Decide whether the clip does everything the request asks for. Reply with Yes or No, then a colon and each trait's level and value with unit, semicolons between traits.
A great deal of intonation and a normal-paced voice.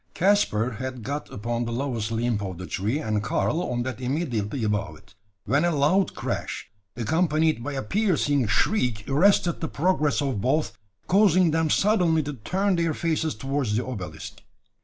Yes: wide, 5.8 semitones; average, 165 wpm